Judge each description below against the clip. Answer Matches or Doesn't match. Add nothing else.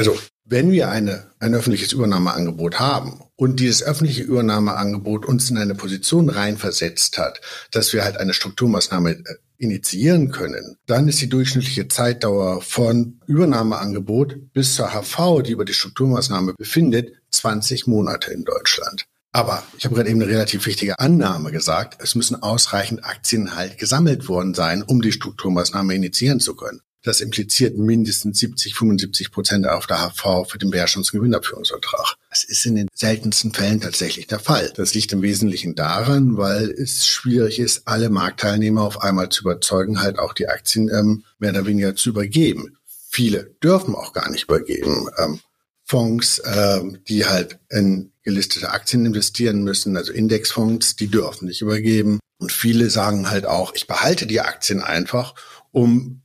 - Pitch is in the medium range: Doesn't match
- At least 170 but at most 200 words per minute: Doesn't match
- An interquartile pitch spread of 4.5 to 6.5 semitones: Doesn't match